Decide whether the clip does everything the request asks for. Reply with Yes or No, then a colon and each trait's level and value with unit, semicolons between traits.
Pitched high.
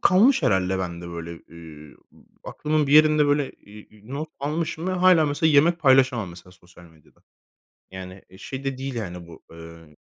No: low, 120 Hz